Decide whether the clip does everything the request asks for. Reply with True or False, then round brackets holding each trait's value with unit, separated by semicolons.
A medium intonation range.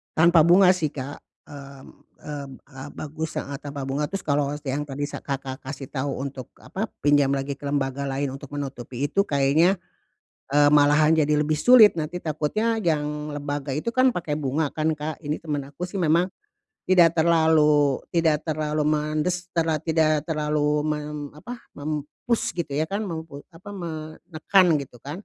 False (2.3 semitones)